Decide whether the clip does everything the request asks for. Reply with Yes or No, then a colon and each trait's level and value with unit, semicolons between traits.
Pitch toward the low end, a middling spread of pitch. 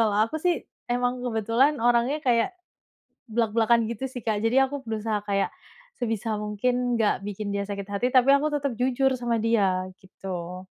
No: high, 230 Hz; average, 3.2 semitones